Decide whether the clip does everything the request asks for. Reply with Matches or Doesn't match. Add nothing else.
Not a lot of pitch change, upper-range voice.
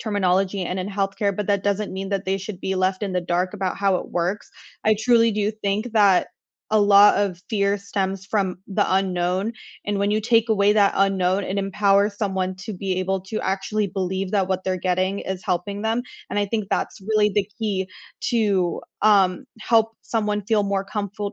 Matches